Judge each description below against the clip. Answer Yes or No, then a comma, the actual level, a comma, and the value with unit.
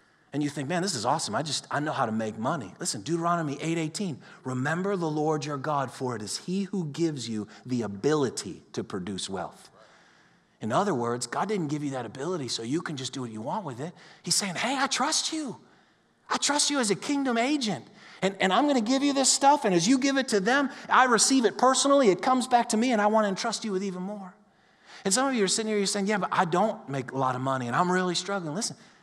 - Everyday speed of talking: No, fast, 255 wpm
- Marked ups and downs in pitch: Yes, wide, 8.1 semitones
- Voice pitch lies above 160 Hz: Yes, high, 190 Hz